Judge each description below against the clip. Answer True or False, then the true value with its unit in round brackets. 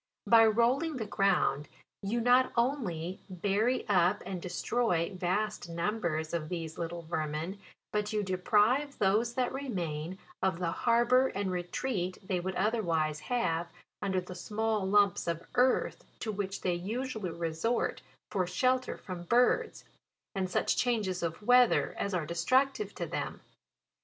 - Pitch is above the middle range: True (195 Hz)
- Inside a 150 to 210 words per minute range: False (140 wpm)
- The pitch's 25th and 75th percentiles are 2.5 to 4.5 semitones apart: False (5.2 semitones)